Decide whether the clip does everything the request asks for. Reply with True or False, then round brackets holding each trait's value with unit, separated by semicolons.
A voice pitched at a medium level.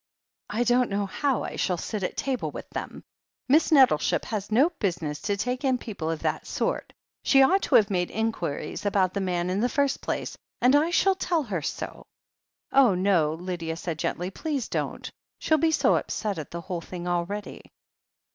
False (205 Hz)